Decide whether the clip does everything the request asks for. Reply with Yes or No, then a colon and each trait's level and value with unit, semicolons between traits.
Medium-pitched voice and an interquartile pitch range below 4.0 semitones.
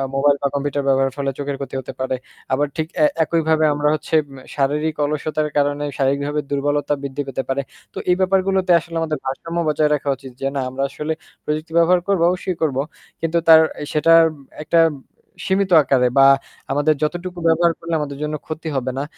Yes: medium, 150 Hz; average, 2.8 semitones